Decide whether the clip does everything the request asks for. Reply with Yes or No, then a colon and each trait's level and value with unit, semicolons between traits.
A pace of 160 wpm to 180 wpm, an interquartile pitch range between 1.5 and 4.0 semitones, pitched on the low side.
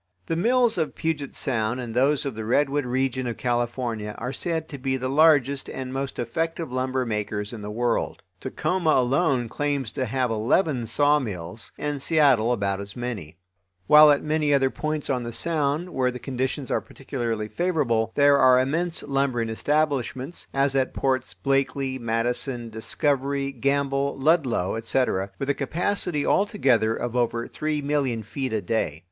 Yes: average, 165 wpm; average, 3.7 semitones; low, 130 Hz